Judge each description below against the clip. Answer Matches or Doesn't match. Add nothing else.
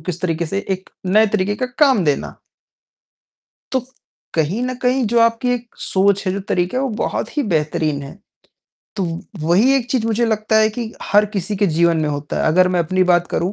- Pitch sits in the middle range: Doesn't match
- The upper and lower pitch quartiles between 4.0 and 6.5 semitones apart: Matches